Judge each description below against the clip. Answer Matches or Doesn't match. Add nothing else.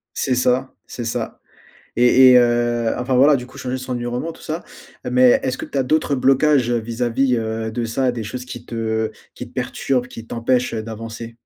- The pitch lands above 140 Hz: Doesn't match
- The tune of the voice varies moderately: Doesn't match